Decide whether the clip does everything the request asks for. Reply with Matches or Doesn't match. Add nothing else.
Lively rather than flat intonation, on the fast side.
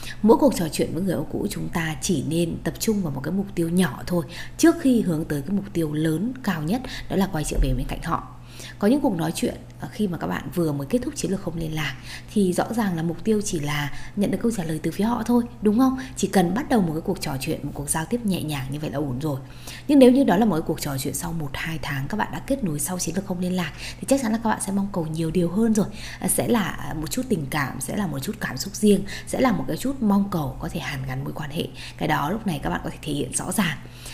Matches